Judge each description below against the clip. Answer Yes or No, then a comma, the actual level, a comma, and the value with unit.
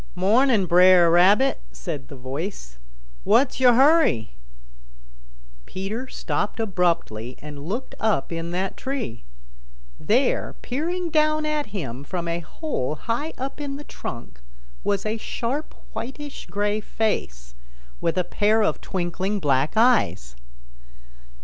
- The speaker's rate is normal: No, slow, 125 wpm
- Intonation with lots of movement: Yes, wide, 7.6 semitones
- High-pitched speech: Yes, high, 200 Hz